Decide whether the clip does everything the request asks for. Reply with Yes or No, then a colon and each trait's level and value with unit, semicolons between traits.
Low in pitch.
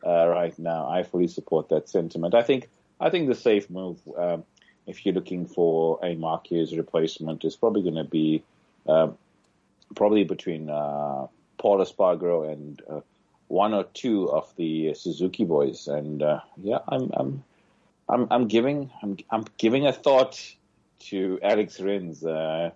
Yes: very low, 85 Hz